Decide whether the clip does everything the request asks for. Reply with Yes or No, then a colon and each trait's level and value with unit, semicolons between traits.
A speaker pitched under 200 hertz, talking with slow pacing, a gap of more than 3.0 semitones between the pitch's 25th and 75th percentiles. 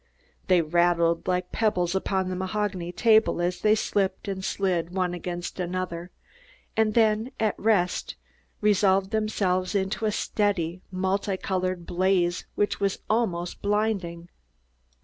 No: high, 190 Hz; slow, 130 wpm; average, 2.7 semitones